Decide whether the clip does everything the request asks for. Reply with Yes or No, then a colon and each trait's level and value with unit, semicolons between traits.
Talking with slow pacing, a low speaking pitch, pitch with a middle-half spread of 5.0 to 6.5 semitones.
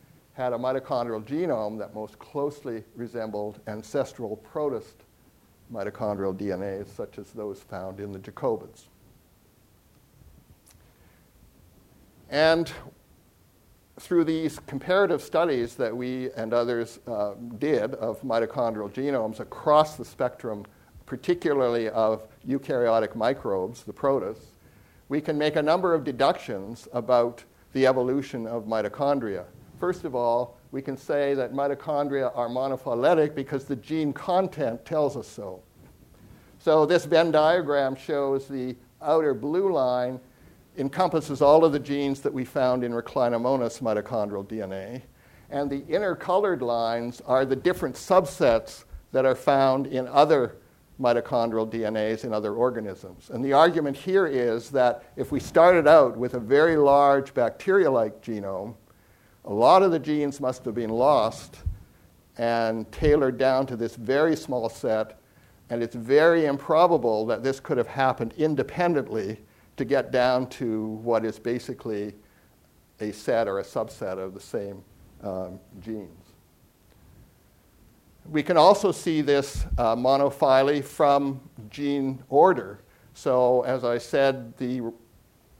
No: slow, 130 wpm; low, 130 Hz; average, 4.0 semitones